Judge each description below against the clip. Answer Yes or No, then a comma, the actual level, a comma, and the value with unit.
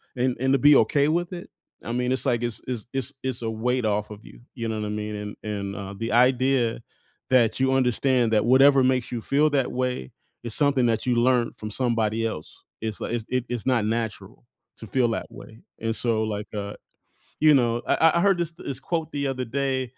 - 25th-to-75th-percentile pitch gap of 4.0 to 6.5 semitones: No, average, 3.1 semitones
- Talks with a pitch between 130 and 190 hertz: No, low, 120 Hz